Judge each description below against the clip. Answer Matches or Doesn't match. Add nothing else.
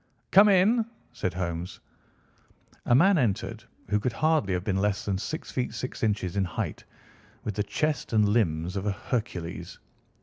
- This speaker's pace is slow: Doesn't match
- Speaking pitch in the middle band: Doesn't match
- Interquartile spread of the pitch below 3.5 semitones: Doesn't match